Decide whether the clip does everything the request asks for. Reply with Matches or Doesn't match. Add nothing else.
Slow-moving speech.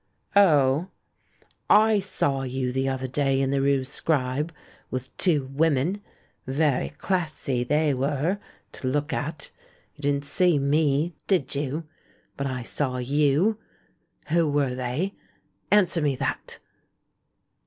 Matches